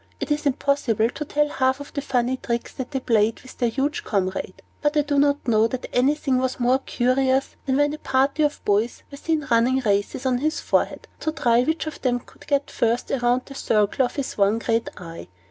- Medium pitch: No, very high, 260 Hz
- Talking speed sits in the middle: No, fast, 215 wpm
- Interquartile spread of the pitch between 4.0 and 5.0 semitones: No, average, 3.4 semitones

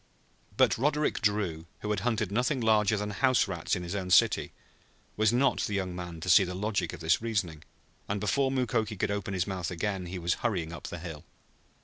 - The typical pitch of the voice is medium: No, low, 100 Hz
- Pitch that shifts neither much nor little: Yes, average, 3.6 semitones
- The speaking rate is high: Yes, fast, 210 wpm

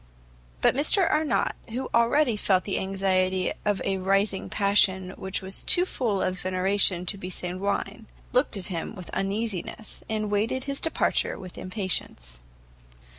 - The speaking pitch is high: Yes, high, 195 Hz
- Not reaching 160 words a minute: Yes, average, 145 wpm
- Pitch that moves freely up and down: No, average, 3.1 semitones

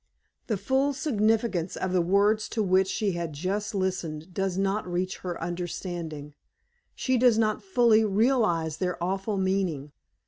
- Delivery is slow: No, average, 145 wpm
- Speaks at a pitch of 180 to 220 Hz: Yes, high, 190 Hz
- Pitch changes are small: No, average, 3.7 semitones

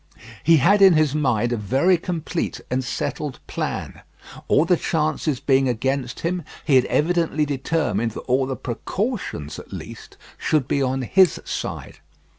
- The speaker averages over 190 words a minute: No, average, 155 wpm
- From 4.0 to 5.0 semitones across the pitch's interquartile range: Yes, average, 4.5 semitones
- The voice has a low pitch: No, medium, 145 Hz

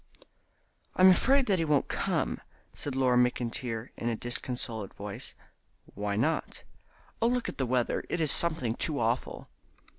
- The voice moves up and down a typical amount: No, wide, 5.7 semitones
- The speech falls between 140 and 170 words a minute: Yes, average, 150 wpm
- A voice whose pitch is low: Yes, low, 125 Hz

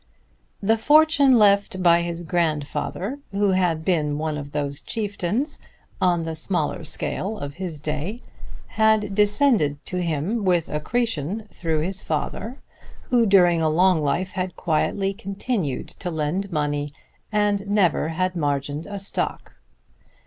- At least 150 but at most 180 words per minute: No, slow, 135 wpm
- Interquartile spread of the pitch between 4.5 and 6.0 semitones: Yes, average, 4.9 semitones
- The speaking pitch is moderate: Yes, medium, 180 Hz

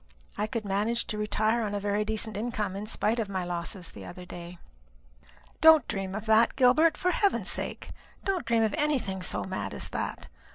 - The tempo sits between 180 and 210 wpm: Yes, average, 195 wpm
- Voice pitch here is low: No, high, 215 Hz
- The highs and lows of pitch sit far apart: No, average, 3.3 semitones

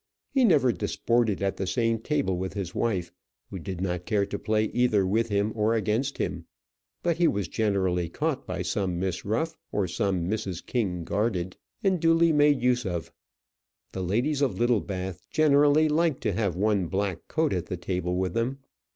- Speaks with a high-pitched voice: No, low, 105 Hz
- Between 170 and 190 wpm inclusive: Yes, average, 180 wpm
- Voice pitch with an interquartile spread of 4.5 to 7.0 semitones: Yes, wide, 5.6 semitones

